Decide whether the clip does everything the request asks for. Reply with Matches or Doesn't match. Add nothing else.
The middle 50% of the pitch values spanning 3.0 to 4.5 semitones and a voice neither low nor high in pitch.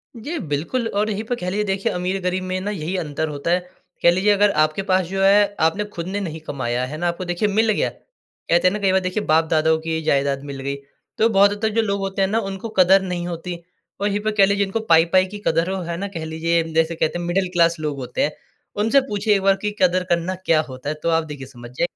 Matches